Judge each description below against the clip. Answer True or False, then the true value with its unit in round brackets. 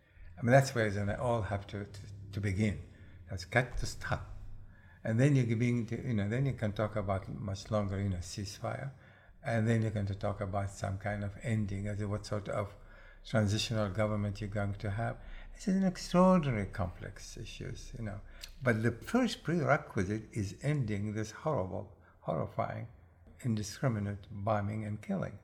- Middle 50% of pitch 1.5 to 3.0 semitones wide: True (2.7 semitones)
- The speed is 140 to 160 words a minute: False (175 wpm)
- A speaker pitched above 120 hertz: False (105 Hz)